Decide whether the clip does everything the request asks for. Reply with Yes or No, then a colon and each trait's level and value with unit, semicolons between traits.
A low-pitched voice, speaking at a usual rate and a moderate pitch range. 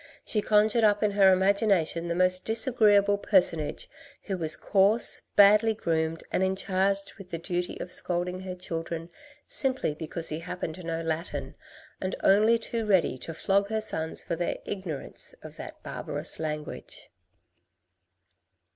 No: medium, 185 Hz; average, 145 wpm; average, 3.6 semitones